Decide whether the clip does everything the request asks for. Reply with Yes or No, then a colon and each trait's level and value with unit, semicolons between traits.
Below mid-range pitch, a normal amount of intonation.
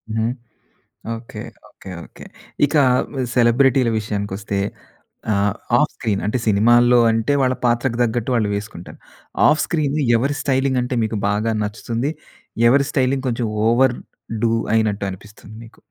Yes: low, 115 Hz; average, 3.4 semitones